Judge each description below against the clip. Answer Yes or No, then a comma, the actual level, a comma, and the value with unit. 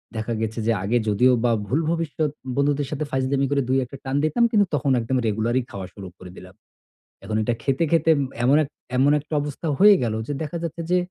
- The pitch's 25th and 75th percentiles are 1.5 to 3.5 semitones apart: No, average, 4.6 semitones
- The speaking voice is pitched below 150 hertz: Yes, low, 135 Hz